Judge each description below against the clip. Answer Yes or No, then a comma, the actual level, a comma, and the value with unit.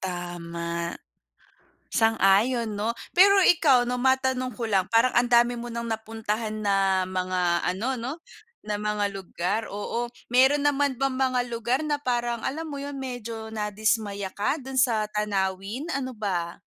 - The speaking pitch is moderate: No, high, 225 Hz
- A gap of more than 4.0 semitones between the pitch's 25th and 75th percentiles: Yes, average, 4.4 semitones